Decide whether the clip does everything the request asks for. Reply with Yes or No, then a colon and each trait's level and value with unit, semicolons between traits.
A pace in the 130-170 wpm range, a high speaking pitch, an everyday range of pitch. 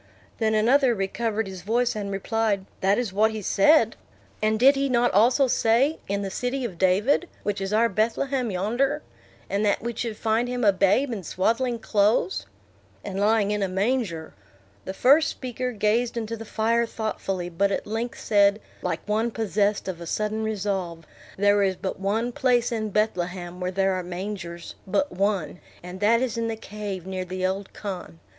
No: average, 180 wpm; high, 210 Hz; average, 3.3 semitones